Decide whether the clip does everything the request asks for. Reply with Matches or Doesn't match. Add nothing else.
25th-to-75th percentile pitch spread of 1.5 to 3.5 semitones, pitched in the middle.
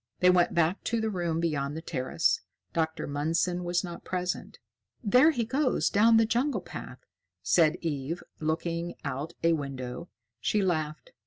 Doesn't match